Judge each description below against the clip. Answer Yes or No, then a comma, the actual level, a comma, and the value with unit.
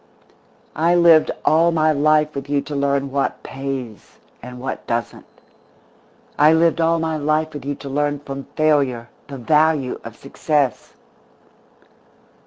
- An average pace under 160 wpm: Yes, average, 145 wpm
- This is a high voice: No, medium, 145 Hz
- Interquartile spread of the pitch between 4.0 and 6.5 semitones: No, narrow, 2.4 semitones